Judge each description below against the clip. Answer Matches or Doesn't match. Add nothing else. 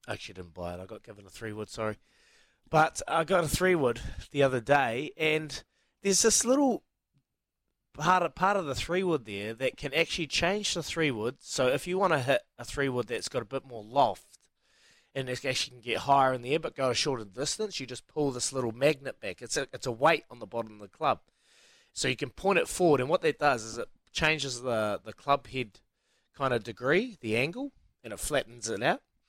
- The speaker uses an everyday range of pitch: Doesn't match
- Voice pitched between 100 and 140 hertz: Matches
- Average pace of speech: Doesn't match